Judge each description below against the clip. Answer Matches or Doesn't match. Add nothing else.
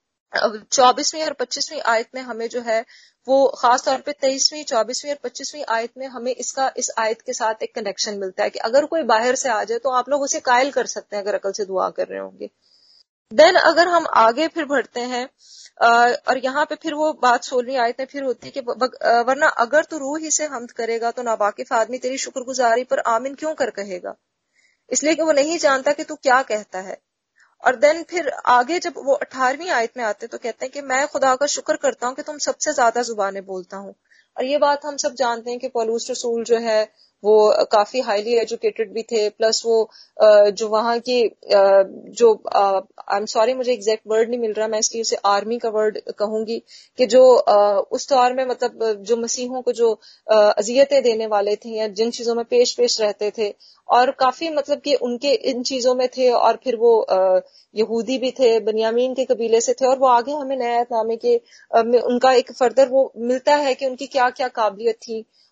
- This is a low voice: Doesn't match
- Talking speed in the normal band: Doesn't match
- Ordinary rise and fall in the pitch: Matches